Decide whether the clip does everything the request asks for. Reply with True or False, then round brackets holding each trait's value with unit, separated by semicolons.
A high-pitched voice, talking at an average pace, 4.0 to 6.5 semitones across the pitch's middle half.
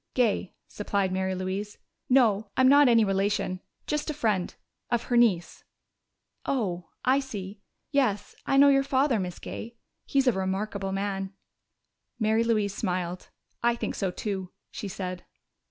True (205 Hz; 150 wpm; 4.3 semitones)